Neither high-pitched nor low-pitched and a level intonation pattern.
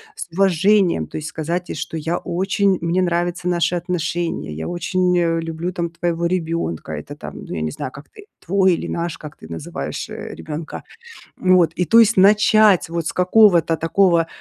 Yes: medium, 170 Hz; narrow, 2.2 semitones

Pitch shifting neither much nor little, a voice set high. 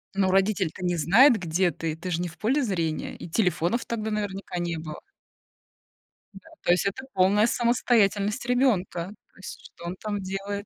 Yes: average, 3.5 semitones; high, 195 Hz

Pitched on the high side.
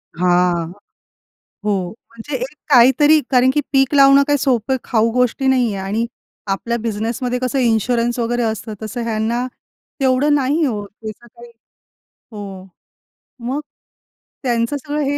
Yes: high, 240 Hz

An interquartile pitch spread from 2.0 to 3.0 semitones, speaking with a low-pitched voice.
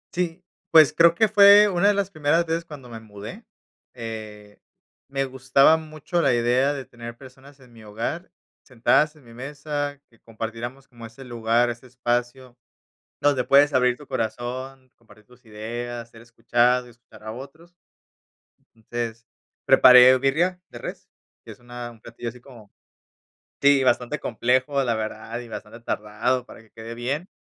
No: average, 3.6 semitones; low, 125 Hz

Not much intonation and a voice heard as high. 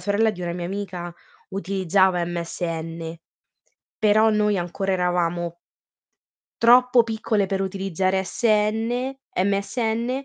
No: average, 3.6 semitones; high, 195 Hz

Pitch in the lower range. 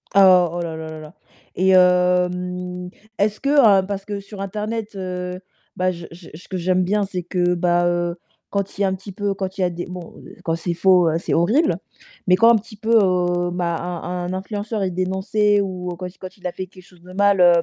No: medium, 185 Hz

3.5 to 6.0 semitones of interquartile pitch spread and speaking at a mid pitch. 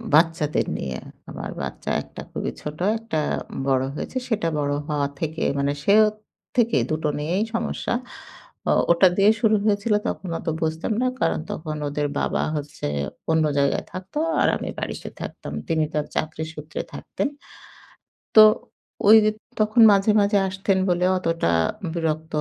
Yes: average, 5.1 semitones; medium, 165 Hz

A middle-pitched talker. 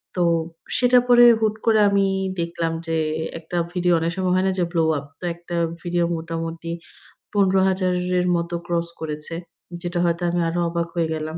Yes: medium, 175 Hz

